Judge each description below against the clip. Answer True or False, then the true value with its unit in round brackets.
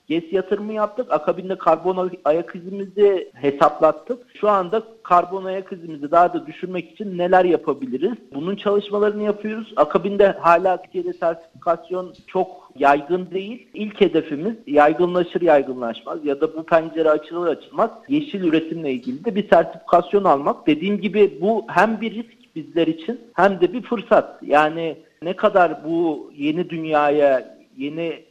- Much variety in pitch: False (4.3 semitones)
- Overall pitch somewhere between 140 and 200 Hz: True (185 Hz)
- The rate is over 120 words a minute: True (140 wpm)